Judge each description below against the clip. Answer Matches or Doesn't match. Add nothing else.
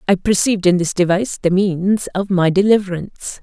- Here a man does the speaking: Doesn't match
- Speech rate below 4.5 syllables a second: Doesn't match